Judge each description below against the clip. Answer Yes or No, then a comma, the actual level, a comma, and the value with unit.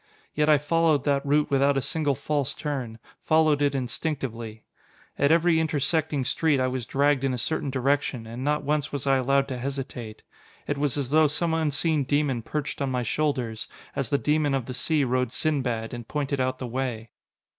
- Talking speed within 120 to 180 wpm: No, average, 190 wpm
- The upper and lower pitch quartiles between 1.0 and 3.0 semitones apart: Yes, average, 2.7 semitones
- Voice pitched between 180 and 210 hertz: No, medium, 140 Hz